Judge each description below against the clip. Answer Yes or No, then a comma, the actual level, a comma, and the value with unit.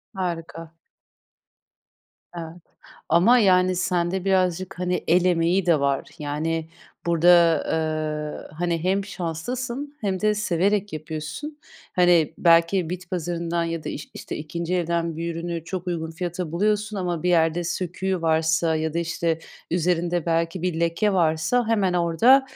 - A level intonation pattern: Yes, narrow, 2.1 semitones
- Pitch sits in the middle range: Yes, medium, 170 Hz